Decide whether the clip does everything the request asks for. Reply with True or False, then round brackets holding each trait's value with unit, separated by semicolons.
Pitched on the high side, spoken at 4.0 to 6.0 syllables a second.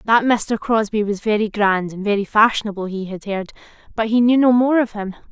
True (215 Hz; 5.5 syllables/s)